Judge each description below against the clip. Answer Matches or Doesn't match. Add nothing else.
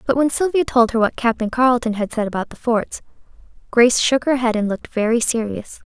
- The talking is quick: Matches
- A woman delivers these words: Matches